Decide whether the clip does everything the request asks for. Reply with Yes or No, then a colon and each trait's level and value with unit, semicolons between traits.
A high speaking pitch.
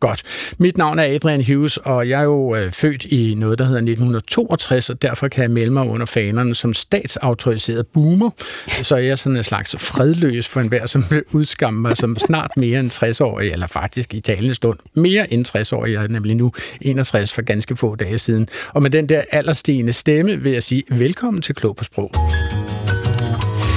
No: low, 125 Hz